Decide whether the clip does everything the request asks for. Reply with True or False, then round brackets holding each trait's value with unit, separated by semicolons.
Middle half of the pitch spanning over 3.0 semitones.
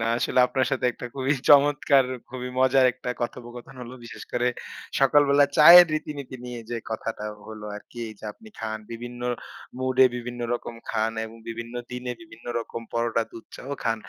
False (2.4 semitones)